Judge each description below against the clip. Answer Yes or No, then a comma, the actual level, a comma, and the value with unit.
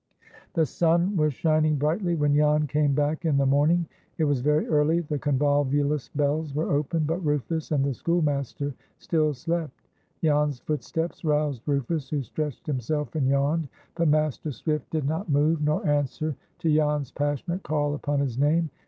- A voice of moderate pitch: Yes, medium, 150 Hz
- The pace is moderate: Yes, average, 165 wpm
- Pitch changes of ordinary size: No, narrow, 1.7 semitones